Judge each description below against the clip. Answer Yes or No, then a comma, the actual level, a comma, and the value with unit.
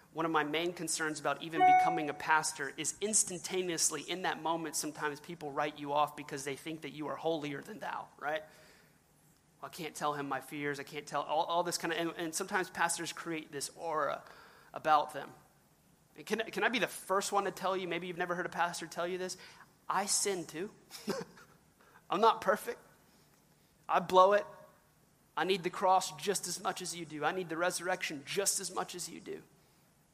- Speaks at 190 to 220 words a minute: Yes, fast, 205 wpm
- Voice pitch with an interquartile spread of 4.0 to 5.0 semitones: No, average, 3.3 semitones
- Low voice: No, medium, 170 Hz